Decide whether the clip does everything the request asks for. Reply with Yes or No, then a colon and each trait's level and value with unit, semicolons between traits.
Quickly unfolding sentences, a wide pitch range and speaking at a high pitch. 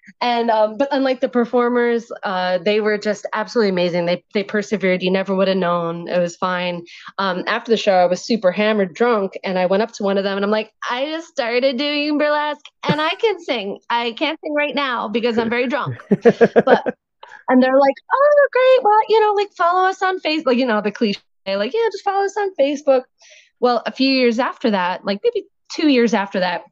Yes: fast, 220 wpm; wide, 6.4 semitones; high, 235 Hz